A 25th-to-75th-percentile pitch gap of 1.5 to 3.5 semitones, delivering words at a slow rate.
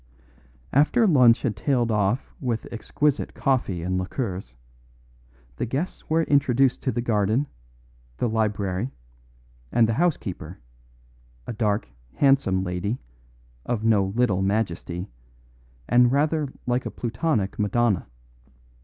No: average, 5.1 semitones; slow, 115 wpm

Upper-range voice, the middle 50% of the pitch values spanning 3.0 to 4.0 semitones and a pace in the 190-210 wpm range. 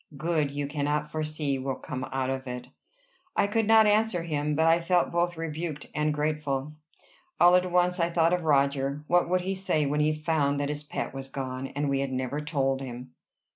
No: medium, 150 Hz; average, 3.5 semitones; fast, 205 wpm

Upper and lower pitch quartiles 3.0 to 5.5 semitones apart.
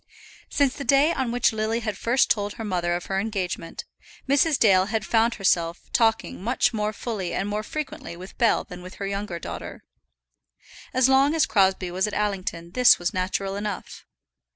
Yes: average, 4.2 semitones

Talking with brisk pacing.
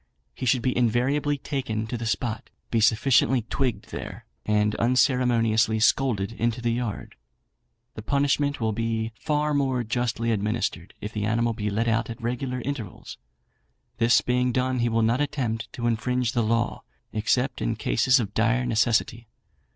No: average, 160 wpm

